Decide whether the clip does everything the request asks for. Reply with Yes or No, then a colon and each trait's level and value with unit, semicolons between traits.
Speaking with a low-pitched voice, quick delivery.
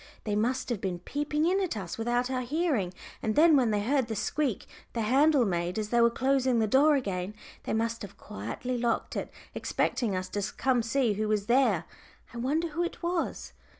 No: high, 240 Hz; fast, 210 wpm